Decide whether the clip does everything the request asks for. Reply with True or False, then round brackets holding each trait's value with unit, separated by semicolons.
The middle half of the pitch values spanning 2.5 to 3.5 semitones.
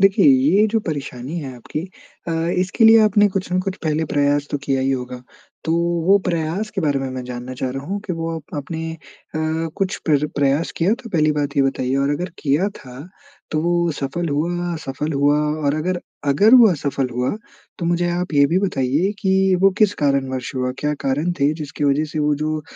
False (4.3 semitones)